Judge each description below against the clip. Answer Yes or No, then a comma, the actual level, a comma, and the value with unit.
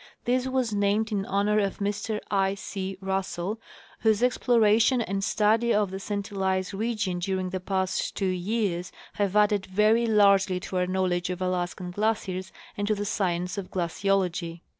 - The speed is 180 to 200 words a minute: No, average, 160 wpm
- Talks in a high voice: Yes, high, 195 Hz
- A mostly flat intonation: Yes, narrow, 2.2 semitones